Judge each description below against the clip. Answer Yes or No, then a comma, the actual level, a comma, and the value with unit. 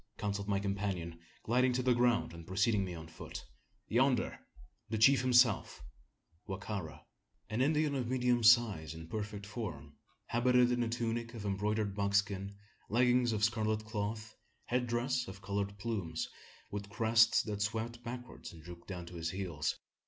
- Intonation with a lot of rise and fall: No, average, 3.5 semitones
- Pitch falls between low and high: No, low, 110 Hz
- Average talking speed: Yes, average, 160 wpm